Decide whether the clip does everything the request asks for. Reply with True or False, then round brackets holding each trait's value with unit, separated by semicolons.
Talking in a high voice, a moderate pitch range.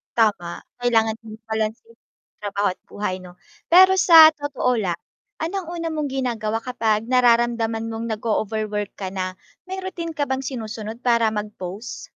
True (225 Hz; 4.0 semitones)